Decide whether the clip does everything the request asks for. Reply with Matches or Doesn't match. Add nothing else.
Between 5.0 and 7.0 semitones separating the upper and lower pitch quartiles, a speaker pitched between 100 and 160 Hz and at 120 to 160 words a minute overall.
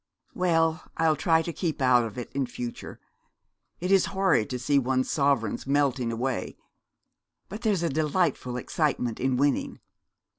Doesn't match